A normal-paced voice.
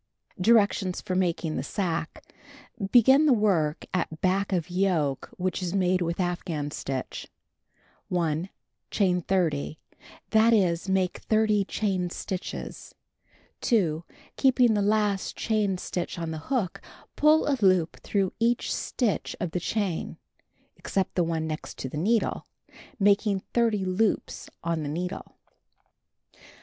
No: slow, 130 wpm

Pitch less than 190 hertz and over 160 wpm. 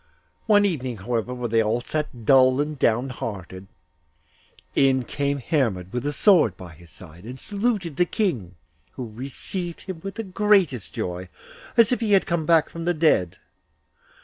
Yes: low, 135 Hz; average, 170 wpm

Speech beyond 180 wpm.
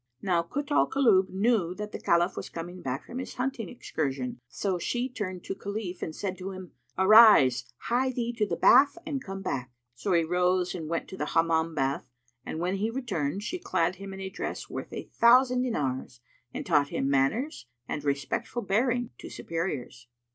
Yes: average, 190 wpm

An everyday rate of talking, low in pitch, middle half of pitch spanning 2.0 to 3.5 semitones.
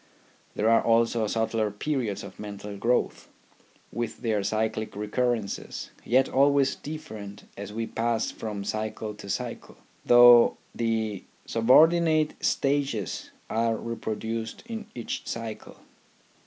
No: slow, 115 wpm; low, 115 Hz; narrow, 2.5 semitones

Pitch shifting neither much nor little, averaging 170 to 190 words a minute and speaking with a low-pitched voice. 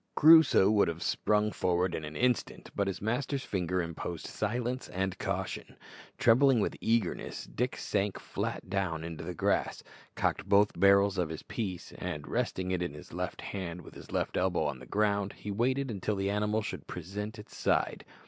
Yes: average, 3.3 semitones; average, 180 wpm; low, 100 Hz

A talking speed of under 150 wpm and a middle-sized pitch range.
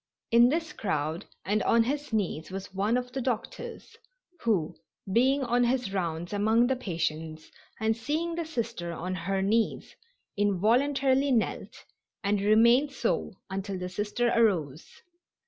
Yes: average, 140 wpm; average, 4.7 semitones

